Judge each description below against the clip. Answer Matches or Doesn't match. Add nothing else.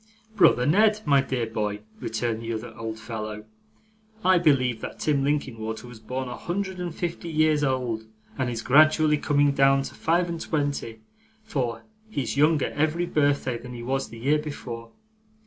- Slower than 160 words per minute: Doesn't match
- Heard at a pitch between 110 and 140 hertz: Matches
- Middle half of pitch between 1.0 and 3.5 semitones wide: Doesn't match